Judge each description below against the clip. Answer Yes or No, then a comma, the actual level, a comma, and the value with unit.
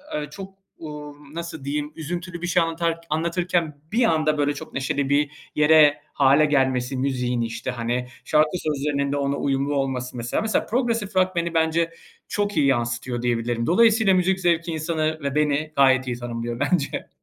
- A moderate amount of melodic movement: Yes, average, 4.0 semitones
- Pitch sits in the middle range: Yes, medium, 150 Hz